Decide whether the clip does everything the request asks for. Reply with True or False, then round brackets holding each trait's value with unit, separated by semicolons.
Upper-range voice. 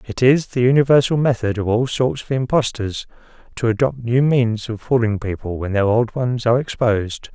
False (120 Hz)